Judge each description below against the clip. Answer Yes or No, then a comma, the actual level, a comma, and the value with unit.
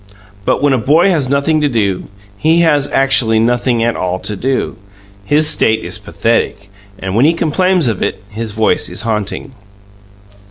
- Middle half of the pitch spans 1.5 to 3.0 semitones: No, wide, 5.4 semitones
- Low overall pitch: Yes, low, 125 Hz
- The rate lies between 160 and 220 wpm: Yes, average, 170 wpm